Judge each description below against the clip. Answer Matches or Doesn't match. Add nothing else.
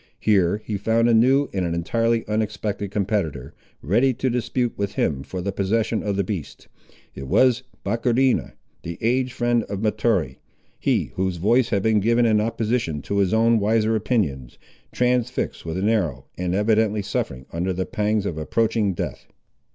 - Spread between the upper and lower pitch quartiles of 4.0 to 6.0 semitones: Doesn't match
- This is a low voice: Matches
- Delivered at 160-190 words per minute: Matches